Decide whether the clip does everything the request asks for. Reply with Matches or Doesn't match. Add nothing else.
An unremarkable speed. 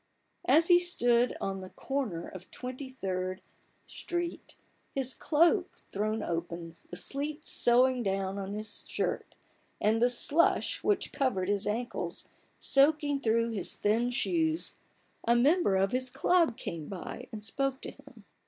Matches